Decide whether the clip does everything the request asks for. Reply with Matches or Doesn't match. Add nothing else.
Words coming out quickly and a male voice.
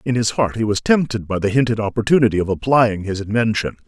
Matches